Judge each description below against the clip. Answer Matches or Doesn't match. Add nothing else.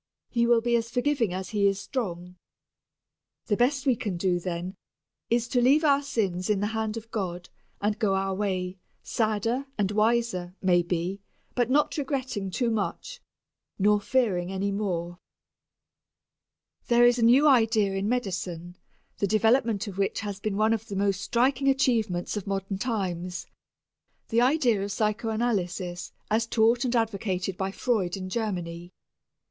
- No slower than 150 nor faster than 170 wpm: Matches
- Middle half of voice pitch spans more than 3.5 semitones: Matches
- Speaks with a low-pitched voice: Doesn't match